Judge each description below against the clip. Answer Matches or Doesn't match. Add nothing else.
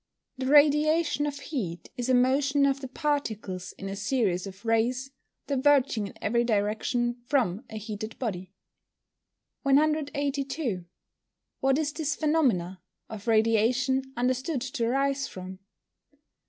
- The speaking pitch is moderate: Doesn't match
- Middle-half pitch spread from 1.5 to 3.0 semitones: Doesn't match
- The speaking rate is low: Matches